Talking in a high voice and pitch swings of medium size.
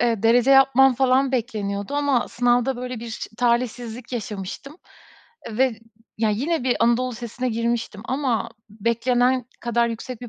No: high, 240 Hz; narrow, 2.0 semitones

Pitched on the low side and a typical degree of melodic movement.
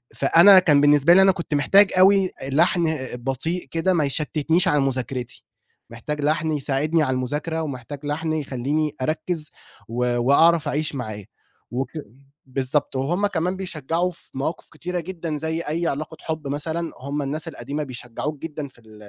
No: medium, 150 Hz; average, 3.5 semitones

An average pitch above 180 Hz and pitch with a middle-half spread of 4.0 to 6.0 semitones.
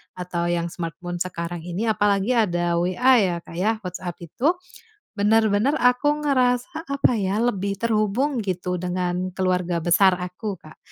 Yes: high, 190 Hz; average, 4.5 semitones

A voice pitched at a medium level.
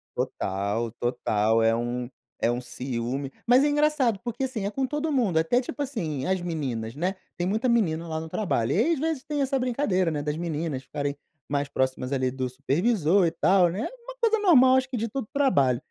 Yes: medium, 175 Hz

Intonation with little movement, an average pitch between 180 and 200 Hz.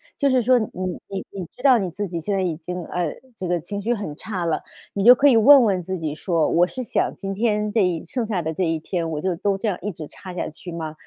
No: average, 4.0 semitones; high, 190 Hz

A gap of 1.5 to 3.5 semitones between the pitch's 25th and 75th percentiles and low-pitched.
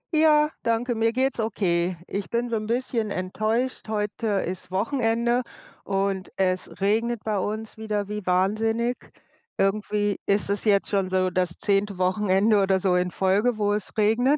No: average, 2.9 semitones; high, 210 Hz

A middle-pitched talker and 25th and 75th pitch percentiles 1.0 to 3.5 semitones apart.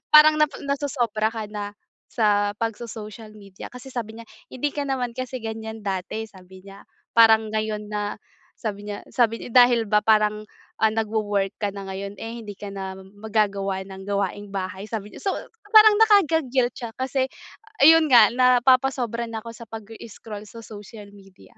No: high, 220 Hz; average, 3.0 semitones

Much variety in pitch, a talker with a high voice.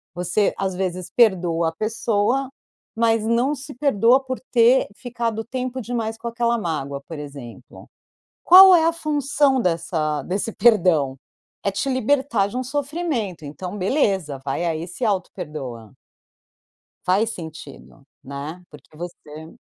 Yes: wide, 7.1 semitones; high, 205 Hz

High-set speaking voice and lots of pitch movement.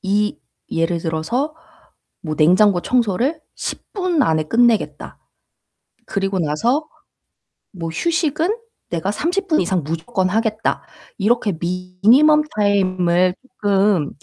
Yes: high, 200 Hz; wide, 6.0 semitones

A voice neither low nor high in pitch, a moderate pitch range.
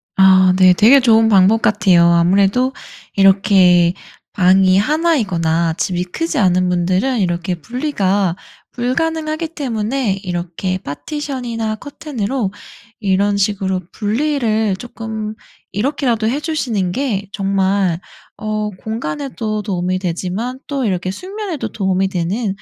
No: high, 205 Hz; average, 5.0 semitones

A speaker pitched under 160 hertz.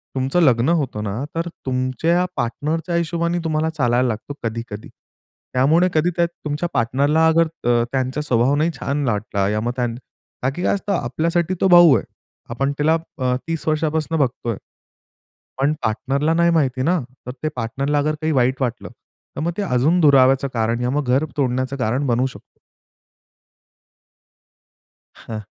Yes: medium, 140 Hz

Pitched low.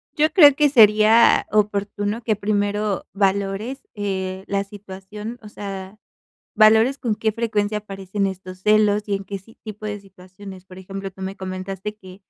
No: high, 205 Hz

